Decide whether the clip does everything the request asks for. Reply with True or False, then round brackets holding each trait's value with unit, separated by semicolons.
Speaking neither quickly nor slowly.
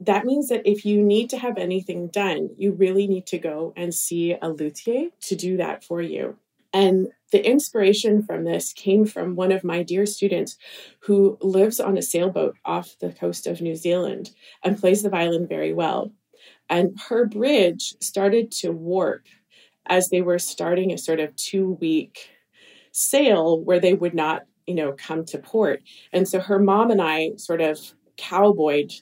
True (180 wpm)